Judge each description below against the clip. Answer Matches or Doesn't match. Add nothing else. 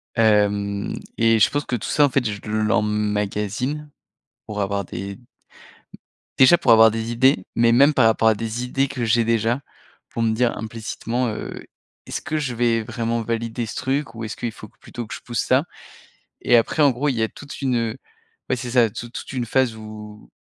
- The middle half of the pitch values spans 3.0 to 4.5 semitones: Doesn't match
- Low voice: Matches